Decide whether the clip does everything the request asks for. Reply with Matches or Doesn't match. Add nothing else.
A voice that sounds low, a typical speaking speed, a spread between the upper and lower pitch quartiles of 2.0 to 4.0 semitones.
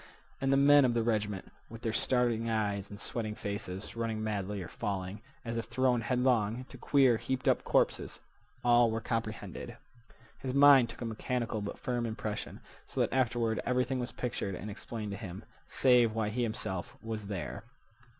Matches